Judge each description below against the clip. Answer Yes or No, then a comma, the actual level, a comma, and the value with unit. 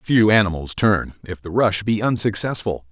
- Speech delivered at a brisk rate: No, average, 165 wpm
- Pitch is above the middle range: No, low, 105 Hz